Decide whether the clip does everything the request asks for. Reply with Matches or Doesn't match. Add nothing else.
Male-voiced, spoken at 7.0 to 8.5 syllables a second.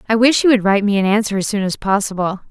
Doesn't match